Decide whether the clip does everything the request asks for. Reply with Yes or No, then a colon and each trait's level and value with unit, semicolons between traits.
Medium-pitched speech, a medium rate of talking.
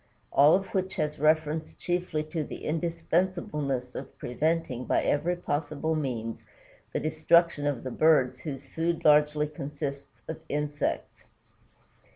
No: medium, 155 Hz; slow, 130 wpm